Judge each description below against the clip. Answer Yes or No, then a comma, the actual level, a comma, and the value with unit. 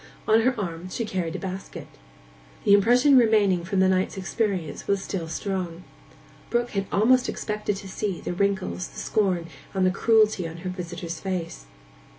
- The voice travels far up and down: No, average, 2.9 semitones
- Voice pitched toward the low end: No, high, 190 Hz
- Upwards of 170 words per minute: No, average, 165 wpm